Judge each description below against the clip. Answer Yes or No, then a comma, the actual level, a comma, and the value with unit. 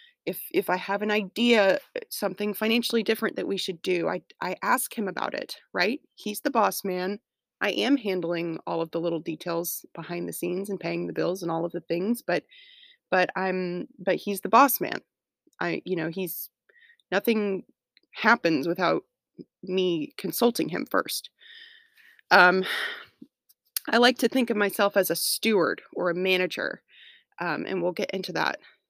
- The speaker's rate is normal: Yes, average, 170 wpm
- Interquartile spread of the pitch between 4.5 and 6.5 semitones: Yes, average, 4.8 semitones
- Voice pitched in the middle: No, high, 195 Hz